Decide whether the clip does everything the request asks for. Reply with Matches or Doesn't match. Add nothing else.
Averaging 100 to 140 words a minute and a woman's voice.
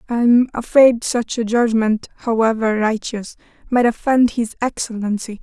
Matches